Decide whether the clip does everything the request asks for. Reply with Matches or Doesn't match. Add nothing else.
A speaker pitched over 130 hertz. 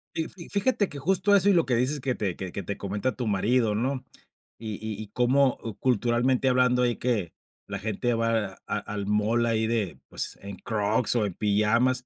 Doesn't match